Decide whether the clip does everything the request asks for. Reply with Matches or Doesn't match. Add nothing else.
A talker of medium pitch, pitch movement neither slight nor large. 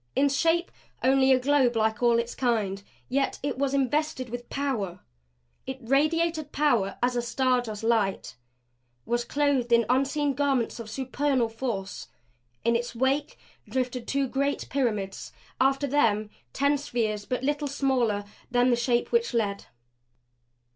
Doesn't match